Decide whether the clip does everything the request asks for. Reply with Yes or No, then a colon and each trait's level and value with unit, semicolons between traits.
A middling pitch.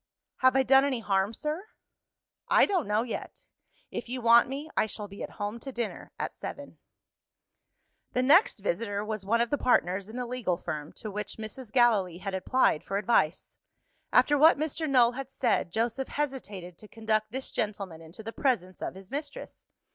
No: high, 230 Hz